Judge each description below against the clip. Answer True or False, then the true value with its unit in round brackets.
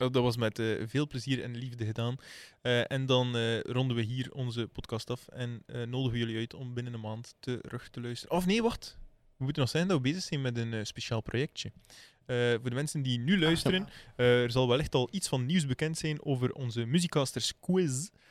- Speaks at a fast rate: True (225 wpm)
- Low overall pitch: True (125 Hz)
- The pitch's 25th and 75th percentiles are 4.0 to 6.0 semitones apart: False (2.9 semitones)